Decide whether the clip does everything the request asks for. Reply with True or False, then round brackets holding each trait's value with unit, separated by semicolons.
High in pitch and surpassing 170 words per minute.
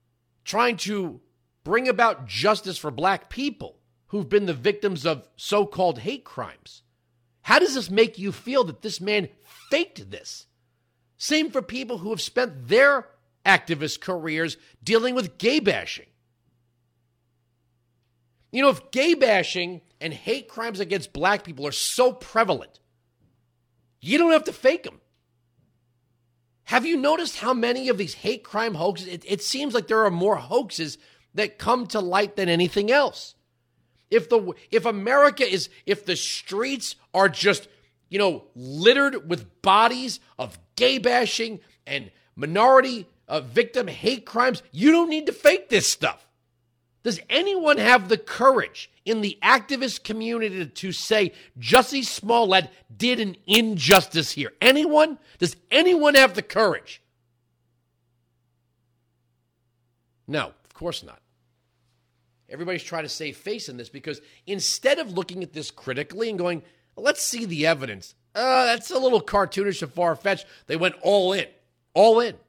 False (195 Hz; 150 wpm)